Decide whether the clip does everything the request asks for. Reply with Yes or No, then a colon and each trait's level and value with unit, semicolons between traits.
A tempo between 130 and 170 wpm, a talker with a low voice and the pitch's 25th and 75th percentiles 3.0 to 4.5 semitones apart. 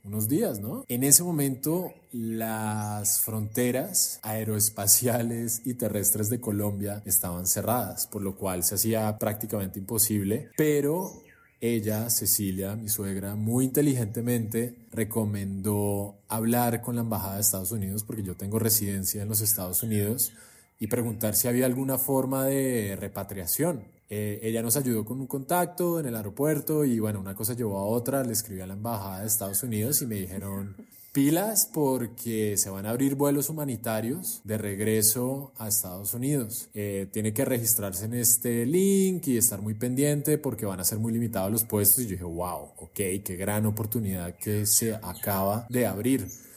Yes: average, 160 wpm; low, 110 Hz; average, 3.3 semitones